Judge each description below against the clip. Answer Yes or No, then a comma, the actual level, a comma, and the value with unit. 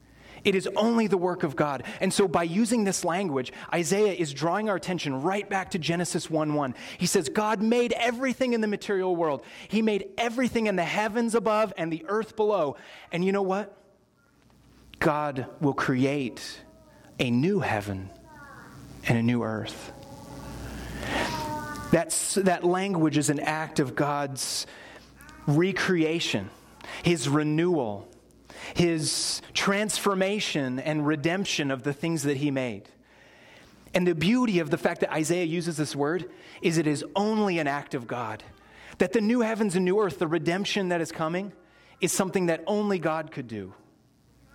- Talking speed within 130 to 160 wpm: Yes, average, 155 wpm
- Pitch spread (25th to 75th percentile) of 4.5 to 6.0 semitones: Yes, average, 5.2 semitones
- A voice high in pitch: No, medium, 170 Hz